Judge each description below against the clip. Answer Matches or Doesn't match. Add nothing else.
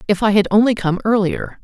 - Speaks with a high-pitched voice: Matches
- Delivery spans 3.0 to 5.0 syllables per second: Doesn't match